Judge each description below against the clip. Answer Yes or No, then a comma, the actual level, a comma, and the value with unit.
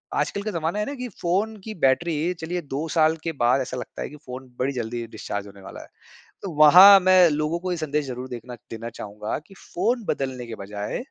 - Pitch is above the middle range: No, medium, 150 Hz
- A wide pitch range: Yes, wide, 6.4 semitones